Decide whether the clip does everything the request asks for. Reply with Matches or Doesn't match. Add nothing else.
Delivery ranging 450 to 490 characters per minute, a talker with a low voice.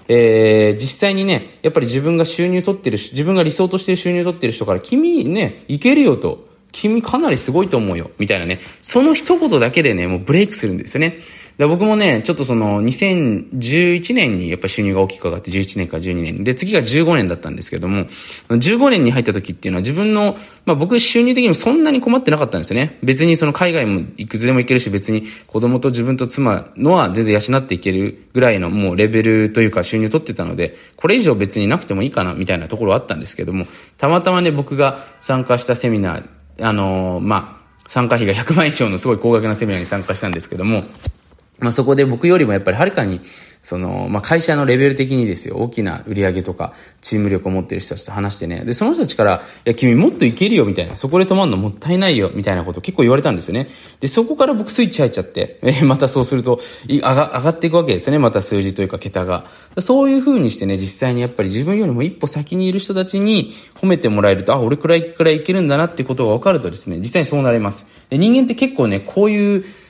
Matches